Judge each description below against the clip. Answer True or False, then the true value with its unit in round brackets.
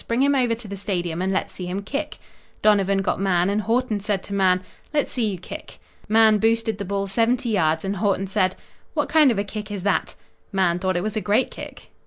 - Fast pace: True (230 wpm)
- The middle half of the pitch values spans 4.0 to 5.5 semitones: False (2.9 semitones)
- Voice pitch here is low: False (200 Hz)